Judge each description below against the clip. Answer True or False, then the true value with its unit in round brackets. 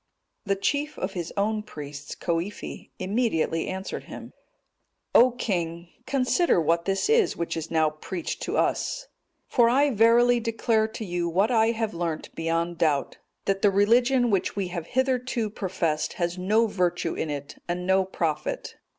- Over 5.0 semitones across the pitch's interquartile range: True (5.4 semitones)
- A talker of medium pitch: False (195 Hz)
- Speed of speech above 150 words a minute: True (160 wpm)